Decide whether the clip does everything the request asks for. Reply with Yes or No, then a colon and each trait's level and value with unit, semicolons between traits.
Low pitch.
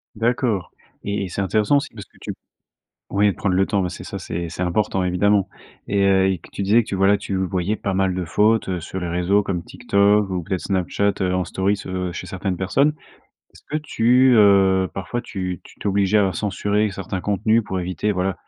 Yes: very low, 95 Hz